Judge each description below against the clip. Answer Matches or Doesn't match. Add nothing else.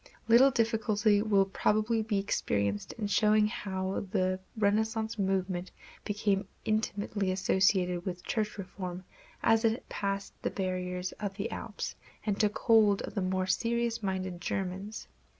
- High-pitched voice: Matches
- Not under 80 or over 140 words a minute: Matches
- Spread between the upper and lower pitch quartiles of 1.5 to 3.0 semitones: Matches